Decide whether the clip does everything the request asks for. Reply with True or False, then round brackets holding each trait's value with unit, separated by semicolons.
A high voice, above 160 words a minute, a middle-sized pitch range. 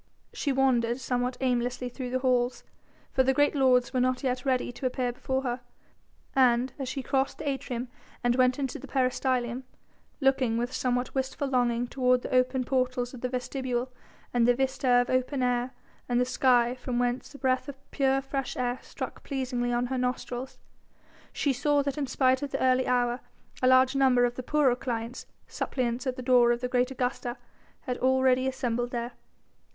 False (255 Hz; 185 wpm; 1.3 semitones)